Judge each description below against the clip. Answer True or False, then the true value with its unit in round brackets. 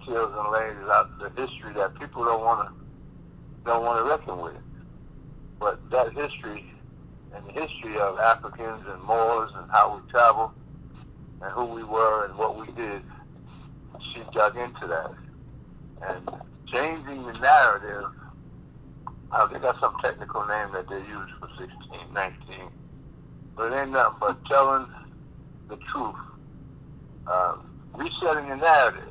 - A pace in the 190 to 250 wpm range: False (140 wpm)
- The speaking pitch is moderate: False (115 Hz)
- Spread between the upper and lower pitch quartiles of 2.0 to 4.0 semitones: True (3.4 semitones)